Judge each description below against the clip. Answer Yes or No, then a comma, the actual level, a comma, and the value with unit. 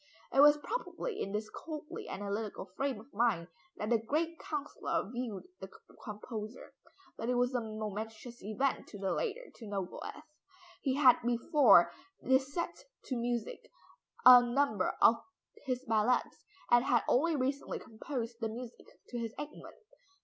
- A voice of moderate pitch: No, high, 240 Hz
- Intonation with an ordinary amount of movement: Yes, average, 4.1 semitones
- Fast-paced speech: No, average, 150 wpm